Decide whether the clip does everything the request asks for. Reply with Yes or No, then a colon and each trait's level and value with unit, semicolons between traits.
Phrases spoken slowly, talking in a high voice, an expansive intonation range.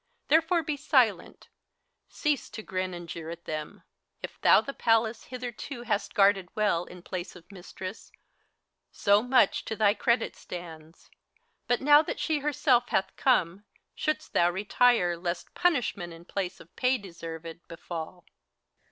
No: average, 145 wpm; high, 200 Hz; wide, 6.1 semitones